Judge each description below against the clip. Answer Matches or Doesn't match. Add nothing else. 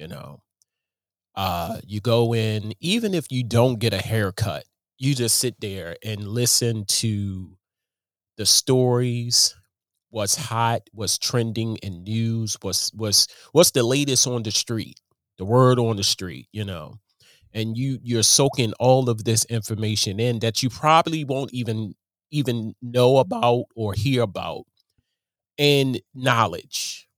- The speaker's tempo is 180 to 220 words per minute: Doesn't match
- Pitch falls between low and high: Doesn't match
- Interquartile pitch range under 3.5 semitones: Matches